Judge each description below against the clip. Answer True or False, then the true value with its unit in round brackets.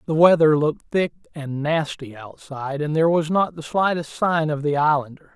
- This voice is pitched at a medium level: True (155 Hz)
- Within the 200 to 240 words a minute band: False (190 wpm)